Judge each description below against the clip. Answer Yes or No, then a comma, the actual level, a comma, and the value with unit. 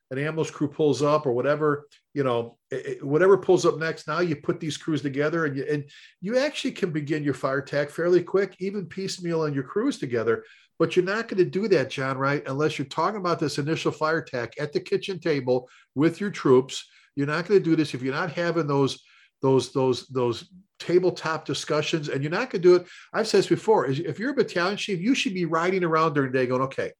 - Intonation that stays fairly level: No, average, 4.2 semitones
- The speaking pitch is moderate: Yes, medium, 160 Hz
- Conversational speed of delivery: No, fast, 230 wpm